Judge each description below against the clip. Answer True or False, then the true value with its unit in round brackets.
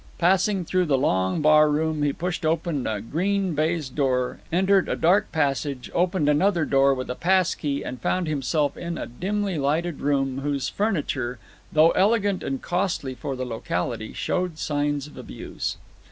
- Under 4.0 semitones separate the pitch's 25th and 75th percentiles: False (4.7 semitones)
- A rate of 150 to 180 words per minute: True (160 wpm)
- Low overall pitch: False (155 Hz)